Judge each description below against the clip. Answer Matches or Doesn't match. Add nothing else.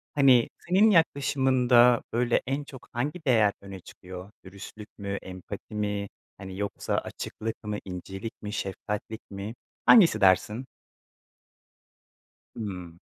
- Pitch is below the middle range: Matches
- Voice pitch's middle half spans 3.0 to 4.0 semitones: Doesn't match